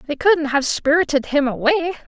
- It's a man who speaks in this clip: No, female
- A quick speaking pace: No, average, 170 wpm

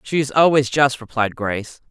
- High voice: No, low, 130 Hz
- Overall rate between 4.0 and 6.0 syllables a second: Yes, 5.1 syllables/s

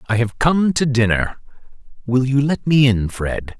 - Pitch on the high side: No, low, 125 Hz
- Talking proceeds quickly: No, average, 185 wpm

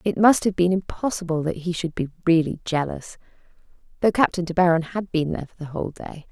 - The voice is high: No, medium, 175 Hz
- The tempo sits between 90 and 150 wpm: No, average, 200 wpm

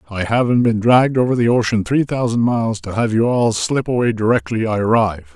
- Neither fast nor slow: No, fast, 215 wpm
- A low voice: Yes, low, 115 Hz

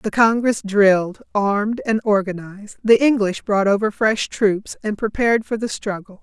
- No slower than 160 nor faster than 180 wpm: Yes, average, 165 wpm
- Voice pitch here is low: No, high, 210 Hz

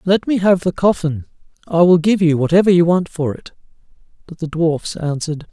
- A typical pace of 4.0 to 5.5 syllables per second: Yes, 5.4 syllables/s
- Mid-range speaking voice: Yes, medium, 170 Hz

